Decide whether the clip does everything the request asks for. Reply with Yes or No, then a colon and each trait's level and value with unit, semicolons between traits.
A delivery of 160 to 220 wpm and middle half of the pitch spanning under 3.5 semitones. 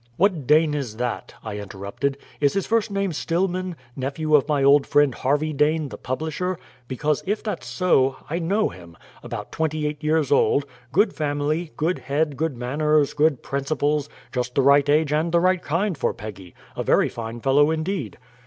Yes: average, 180 wpm; average, 3.1 semitones